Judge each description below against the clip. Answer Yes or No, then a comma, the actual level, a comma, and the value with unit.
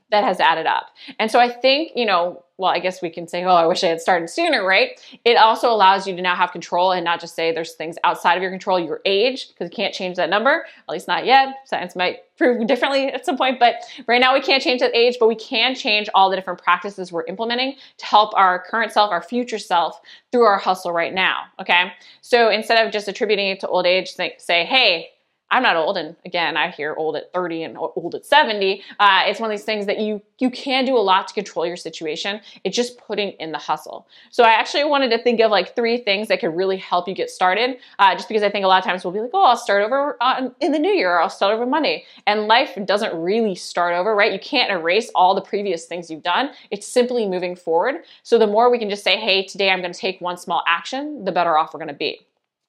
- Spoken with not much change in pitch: No, average, 5.2 semitones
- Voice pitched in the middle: No, high, 205 Hz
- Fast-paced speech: Yes, fast, 260 wpm